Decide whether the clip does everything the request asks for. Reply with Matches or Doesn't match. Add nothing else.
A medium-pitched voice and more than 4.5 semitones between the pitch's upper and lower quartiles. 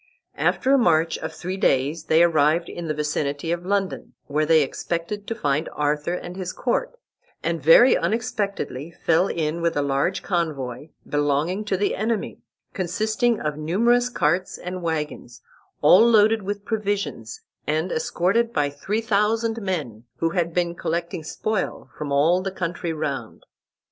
Matches